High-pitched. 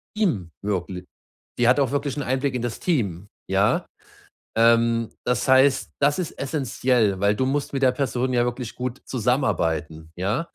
No: low, 125 Hz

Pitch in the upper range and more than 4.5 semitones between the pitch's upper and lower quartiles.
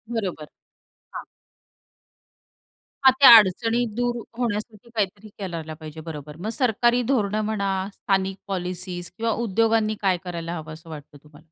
Yes: high, 195 Hz; average, 5.1 semitones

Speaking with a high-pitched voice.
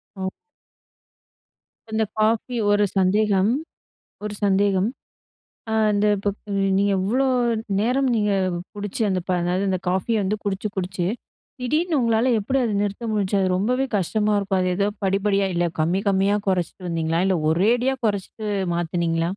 Yes: high, 200 Hz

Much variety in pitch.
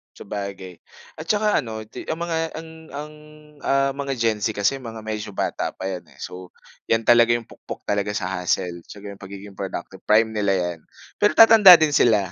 Yes: wide, 5.8 semitones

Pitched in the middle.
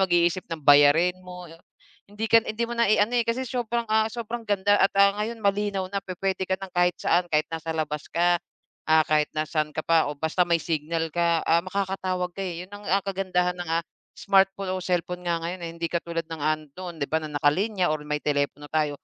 Yes: medium, 180 Hz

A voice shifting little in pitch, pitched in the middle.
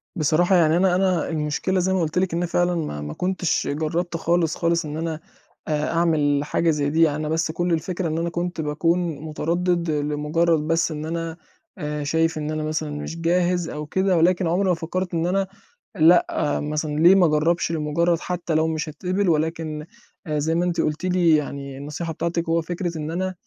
Yes: narrow, 2.3 semitones; medium, 165 Hz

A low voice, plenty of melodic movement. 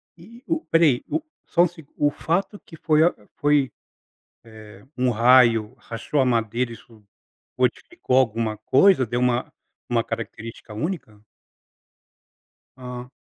Yes: low, 125 Hz; wide, 5.7 semitones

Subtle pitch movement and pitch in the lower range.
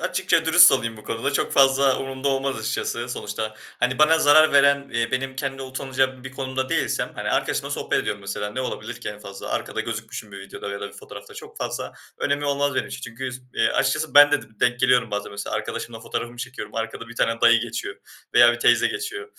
No: average, 3.3 semitones; low, 125 Hz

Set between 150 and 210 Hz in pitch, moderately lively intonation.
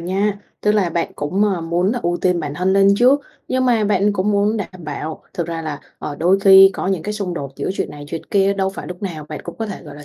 Yes: high, 190 Hz; average, 3.5 semitones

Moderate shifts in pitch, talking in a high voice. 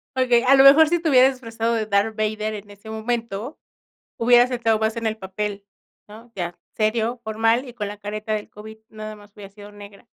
No: narrow, 2.3 semitones; high, 220 Hz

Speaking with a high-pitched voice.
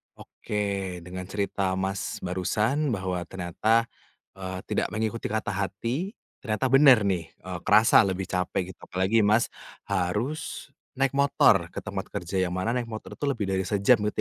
No: low, 100 Hz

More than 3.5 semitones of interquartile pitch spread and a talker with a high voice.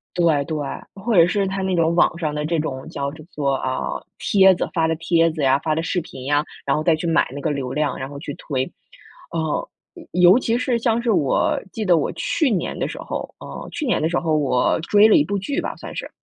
No: average, 4.7 semitones; medium, 165 Hz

